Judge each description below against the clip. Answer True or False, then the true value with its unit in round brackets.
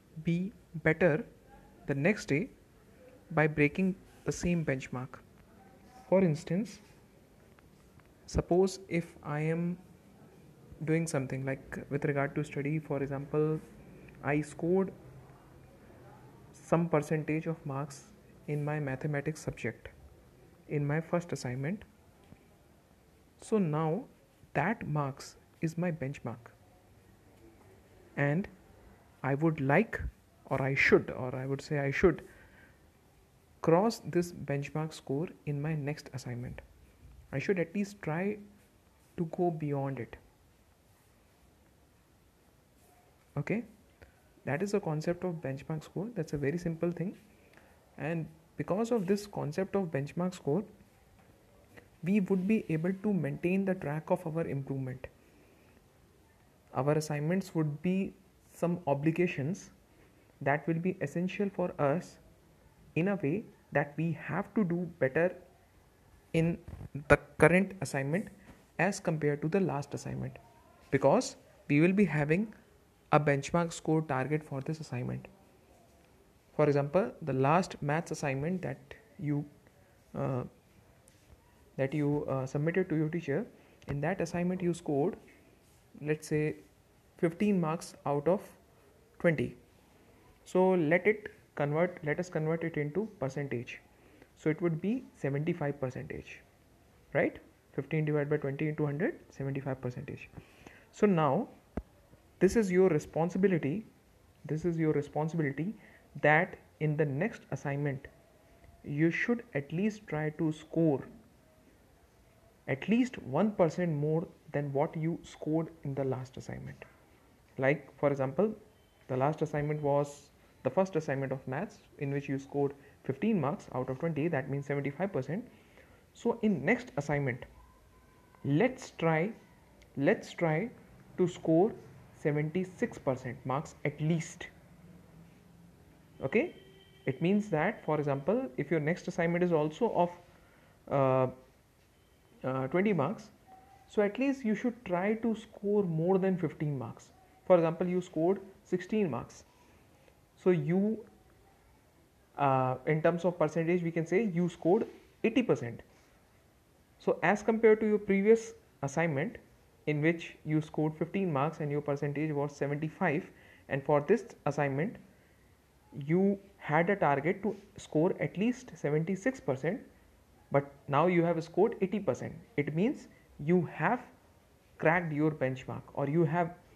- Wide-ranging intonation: False (4.5 semitones)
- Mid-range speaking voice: True (155 Hz)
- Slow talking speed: True (130 wpm)